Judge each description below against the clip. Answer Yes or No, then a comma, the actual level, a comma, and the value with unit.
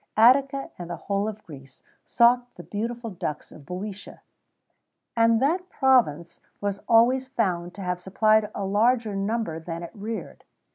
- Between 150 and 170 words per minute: Yes, average, 155 wpm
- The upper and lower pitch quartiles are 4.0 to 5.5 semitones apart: Yes, average, 4.8 semitones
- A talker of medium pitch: No, high, 215 Hz